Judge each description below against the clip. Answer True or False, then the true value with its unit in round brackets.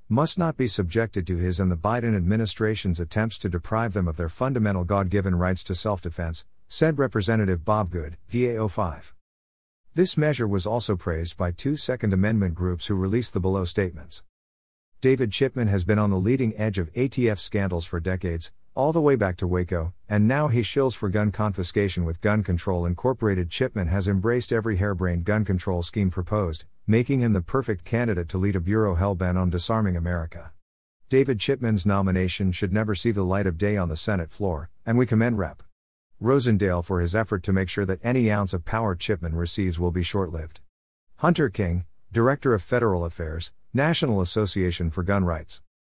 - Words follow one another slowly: False (180 wpm)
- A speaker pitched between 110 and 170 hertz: False (100 Hz)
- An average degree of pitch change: True (4.1 semitones)